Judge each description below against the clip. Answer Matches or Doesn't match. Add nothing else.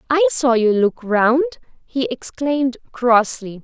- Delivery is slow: Matches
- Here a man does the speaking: Doesn't match